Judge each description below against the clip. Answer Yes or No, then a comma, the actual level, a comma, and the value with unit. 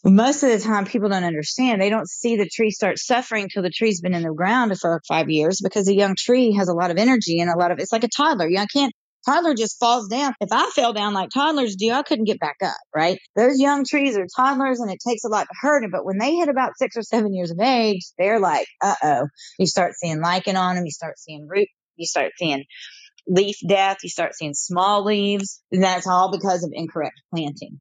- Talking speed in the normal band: No, fast, 250 wpm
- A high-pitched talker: Yes, high, 200 Hz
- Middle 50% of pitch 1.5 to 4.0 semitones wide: No, average, 4.9 semitones